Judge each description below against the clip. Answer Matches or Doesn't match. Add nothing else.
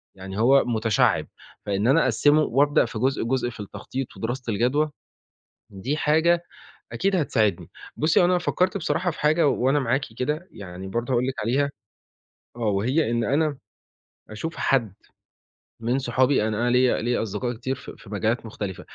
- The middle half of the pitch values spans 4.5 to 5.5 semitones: Matches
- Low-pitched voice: Matches